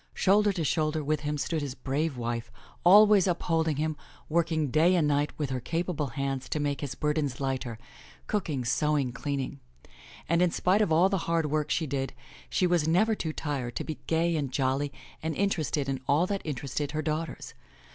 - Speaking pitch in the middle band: Yes, medium, 155 Hz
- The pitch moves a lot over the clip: No, average, 3.3 semitones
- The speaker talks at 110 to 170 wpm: No, average, 185 wpm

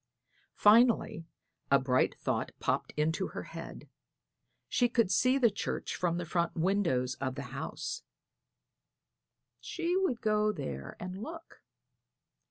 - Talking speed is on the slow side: Yes, slow, 130 wpm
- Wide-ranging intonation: Yes, wide, 7.4 semitones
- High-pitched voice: Yes, high, 195 Hz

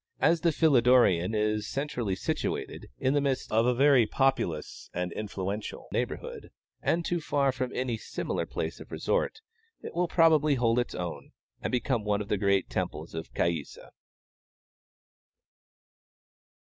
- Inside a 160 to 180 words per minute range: No, average, 145 wpm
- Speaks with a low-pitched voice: Yes, low, 120 Hz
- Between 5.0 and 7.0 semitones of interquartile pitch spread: Yes, wide, 5.5 semitones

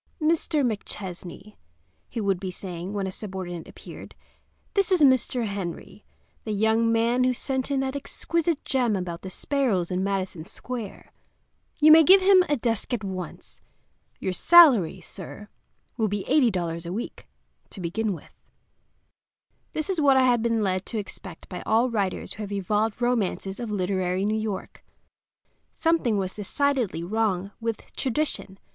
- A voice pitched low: No, high, 215 Hz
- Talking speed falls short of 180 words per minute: Yes, average, 155 wpm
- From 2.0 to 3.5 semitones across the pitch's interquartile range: No, average, 5.2 semitones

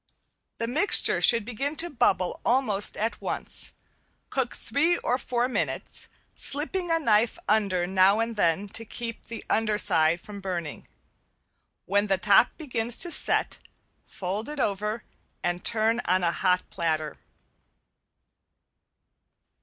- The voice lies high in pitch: Yes, high, 215 Hz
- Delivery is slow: Yes, slow, 130 wpm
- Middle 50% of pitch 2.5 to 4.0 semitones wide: No, average, 4.5 semitones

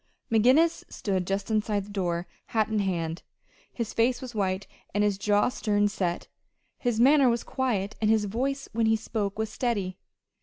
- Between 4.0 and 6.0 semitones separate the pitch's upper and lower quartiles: No, average, 3.1 semitones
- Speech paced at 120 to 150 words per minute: No, average, 175 wpm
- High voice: Yes, high, 215 Hz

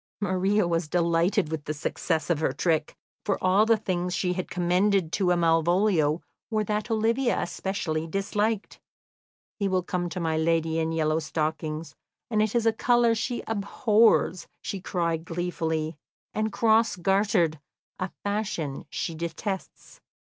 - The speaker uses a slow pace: No, average, 145 wpm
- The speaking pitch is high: No, medium, 180 Hz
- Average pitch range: Yes, average, 4.3 semitones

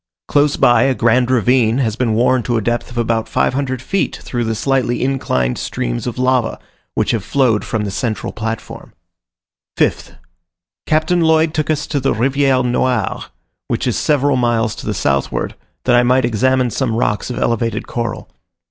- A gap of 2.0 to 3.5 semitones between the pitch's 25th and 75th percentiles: Yes, average, 2.8 semitones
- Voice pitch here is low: Yes, low, 120 Hz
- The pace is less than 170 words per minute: No, average, 175 wpm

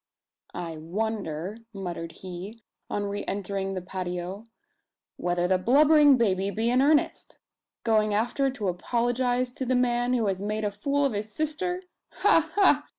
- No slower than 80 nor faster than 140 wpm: No, average, 150 wpm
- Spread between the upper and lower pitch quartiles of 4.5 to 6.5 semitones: Yes, average, 5.2 semitones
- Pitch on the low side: No, high, 215 Hz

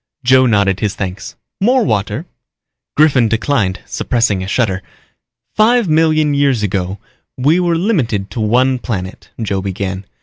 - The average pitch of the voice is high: No, low, 115 Hz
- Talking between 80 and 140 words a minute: Yes, slow, 135 wpm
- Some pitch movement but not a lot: No, wide, 7.1 semitones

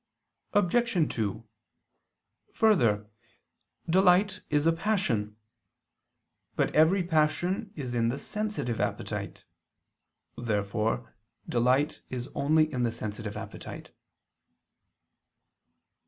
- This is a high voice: No, medium, 145 Hz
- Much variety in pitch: Yes, wide, 7.9 semitones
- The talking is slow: Yes, slow, 85 wpm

